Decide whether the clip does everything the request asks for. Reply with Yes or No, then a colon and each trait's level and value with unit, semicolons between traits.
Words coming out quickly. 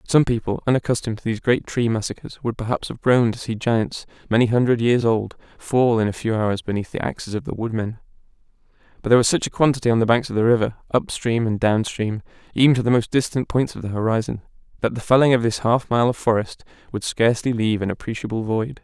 Yes: fast, 225 wpm